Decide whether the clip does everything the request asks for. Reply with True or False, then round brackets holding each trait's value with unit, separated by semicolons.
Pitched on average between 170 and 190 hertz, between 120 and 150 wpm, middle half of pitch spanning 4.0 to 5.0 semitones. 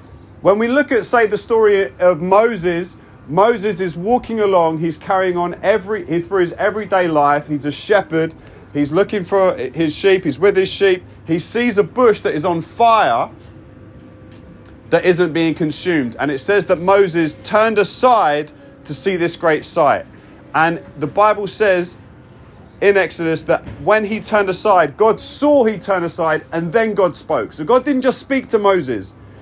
False (185 Hz; 175 wpm; 4.5 semitones)